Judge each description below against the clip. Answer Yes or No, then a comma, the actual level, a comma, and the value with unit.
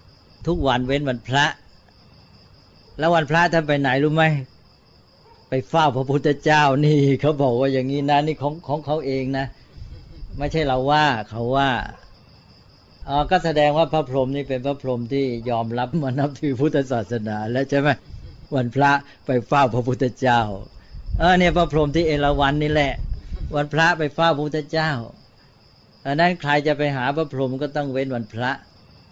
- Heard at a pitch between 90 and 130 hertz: No, medium, 140 Hz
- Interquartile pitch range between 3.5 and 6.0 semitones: No, average, 2.8 semitones